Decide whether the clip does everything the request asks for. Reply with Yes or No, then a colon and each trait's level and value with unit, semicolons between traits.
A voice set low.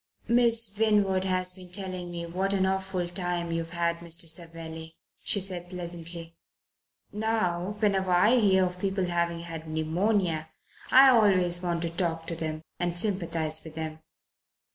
No: medium, 175 Hz